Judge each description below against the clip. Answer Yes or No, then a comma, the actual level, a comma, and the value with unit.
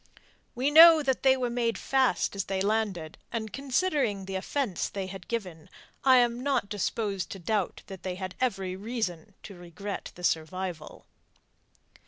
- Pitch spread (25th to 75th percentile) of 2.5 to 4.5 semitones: No, average, 4.9 semitones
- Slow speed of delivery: No, average, 160 wpm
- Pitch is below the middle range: No, high, 205 Hz